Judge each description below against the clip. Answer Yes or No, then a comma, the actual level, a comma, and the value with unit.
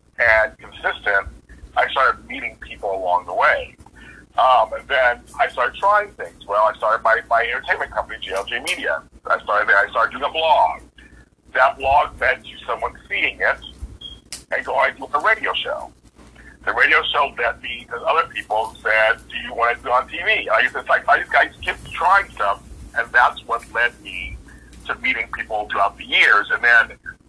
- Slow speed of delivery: No, average, 190 wpm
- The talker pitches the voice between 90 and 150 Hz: No, very low, 75 Hz